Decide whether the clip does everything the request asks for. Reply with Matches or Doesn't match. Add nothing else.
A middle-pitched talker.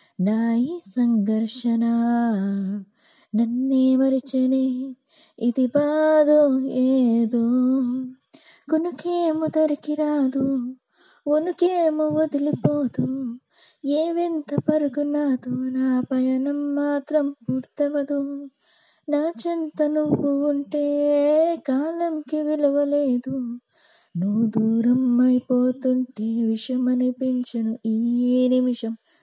Doesn't match